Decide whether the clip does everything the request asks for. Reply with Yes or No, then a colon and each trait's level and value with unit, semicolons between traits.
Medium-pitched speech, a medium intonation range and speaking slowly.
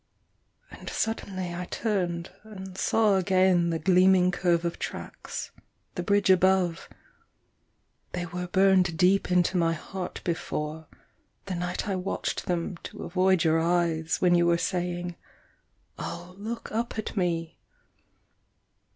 No: medium, 180 Hz; narrow, 1.7 semitones; slow, 130 wpm